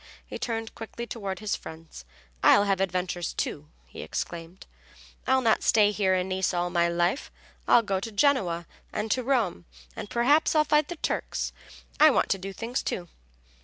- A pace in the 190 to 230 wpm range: No, average, 175 wpm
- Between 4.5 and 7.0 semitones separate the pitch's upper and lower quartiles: Yes, average, 5.0 semitones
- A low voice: No, high, 200 Hz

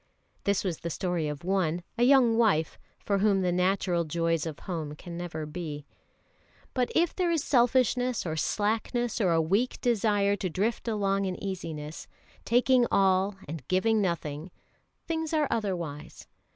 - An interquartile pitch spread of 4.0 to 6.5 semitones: Yes, wide, 5.5 semitones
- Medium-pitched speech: No, high, 195 Hz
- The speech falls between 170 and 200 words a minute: No, average, 155 wpm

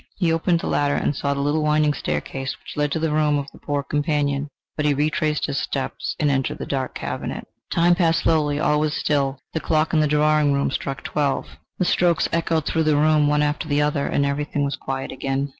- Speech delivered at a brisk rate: Yes, fast, 225 wpm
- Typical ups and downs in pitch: No, narrow, 1.6 semitones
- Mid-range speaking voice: Yes, medium, 150 Hz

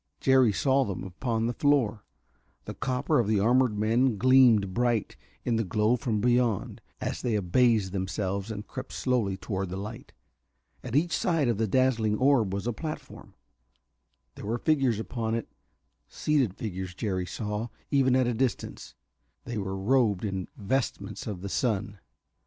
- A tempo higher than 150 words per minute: Yes, average, 160 wpm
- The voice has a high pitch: No, low, 115 Hz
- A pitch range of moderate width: Yes, average, 4.0 semitones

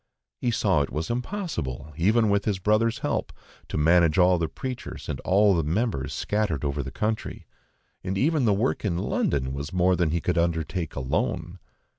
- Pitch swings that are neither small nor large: No, wide, 5.8 semitones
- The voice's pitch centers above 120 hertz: No, very low, 90 Hz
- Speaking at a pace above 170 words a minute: Yes, average, 180 wpm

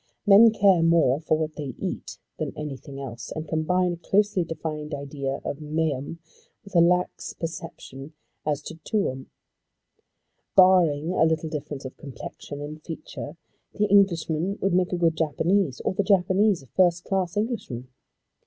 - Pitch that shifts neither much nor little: Yes, average, 3.9 semitones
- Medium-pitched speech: Yes, medium, 160 Hz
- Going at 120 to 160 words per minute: Yes, average, 155 wpm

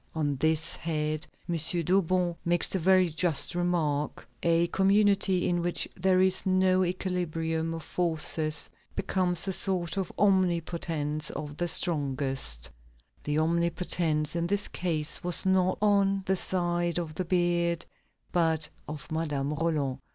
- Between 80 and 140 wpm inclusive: Yes, slow, 135 wpm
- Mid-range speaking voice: Yes, medium, 170 Hz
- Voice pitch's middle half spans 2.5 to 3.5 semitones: Yes, average, 2.8 semitones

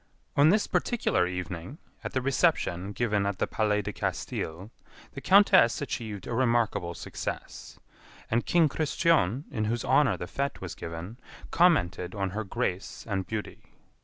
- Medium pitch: No, low, 110 Hz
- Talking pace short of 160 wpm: Yes, average, 150 wpm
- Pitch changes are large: Yes, wide, 6.8 semitones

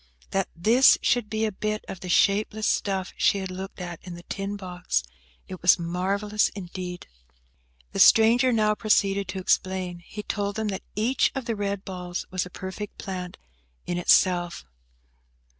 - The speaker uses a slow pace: No, average, 160 wpm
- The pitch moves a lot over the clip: No, average, 2.8 semitones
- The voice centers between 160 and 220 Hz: Yes, high, 190 Hz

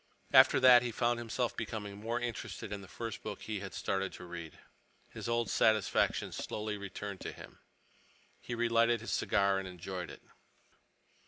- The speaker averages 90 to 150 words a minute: No, average, 165 wpm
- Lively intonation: No, average, 3.2 semitones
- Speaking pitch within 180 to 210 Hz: No, low, 110 Hz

